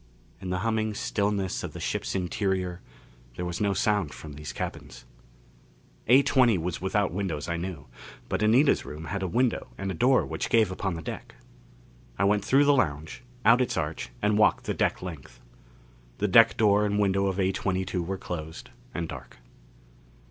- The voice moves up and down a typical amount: Yes, average, 3.3 semitones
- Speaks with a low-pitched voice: Yes, very low, 95 Hz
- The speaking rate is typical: Yes, average, 175 wpm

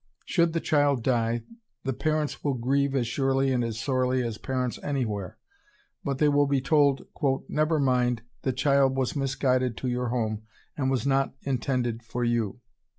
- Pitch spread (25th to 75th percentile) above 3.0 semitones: No, narrow, 2.4 semitones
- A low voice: Yes, low, 130 Hz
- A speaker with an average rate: Yes, average, 170 wpm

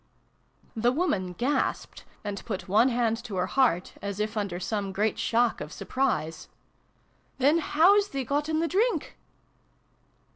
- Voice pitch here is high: Yes, high, 230 Hz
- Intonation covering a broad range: Yes, wide, 6.1 semitones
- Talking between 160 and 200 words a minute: No, average, 150 wpm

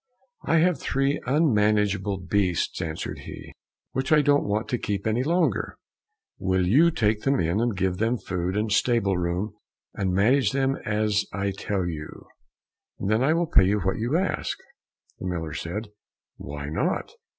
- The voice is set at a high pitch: No, low, 105 Hz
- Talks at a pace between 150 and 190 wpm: Yes, average, 165 wpm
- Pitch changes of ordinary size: No, wide, 5.9 semitones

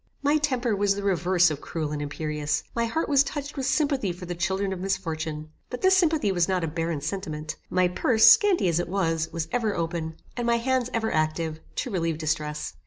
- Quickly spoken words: Yes, fast, 210 wpm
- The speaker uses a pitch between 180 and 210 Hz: Yes, medium, 185 Hz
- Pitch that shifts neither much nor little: No, wide, 6.7 semitones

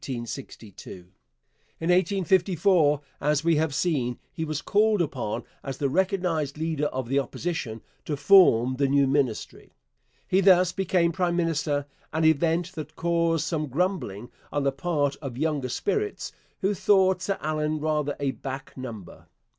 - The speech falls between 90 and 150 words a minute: Yes, average, 145 wpm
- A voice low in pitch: No, medium, 155 Hz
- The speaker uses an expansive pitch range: No, average, 4.4 semitones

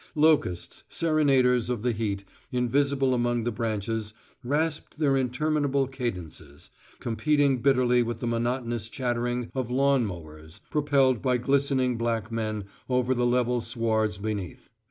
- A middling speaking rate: No, slow, 130 wpm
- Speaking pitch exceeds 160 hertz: No, low, 120 Hz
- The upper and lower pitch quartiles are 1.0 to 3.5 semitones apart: Yes, average, 3.1 semitones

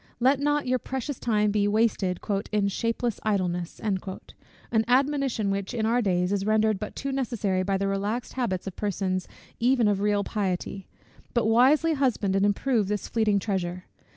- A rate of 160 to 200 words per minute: Yes, average, 165 wpm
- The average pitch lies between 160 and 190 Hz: No, high, 210 Hz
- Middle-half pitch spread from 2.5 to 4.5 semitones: Yes, average, 3.7 semitones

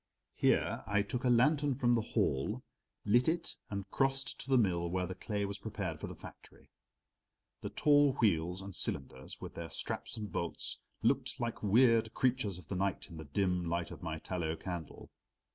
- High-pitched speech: No, low, 100 Hz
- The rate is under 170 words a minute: No, average, 185 wpm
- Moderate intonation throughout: No, wide, 5.8 semitones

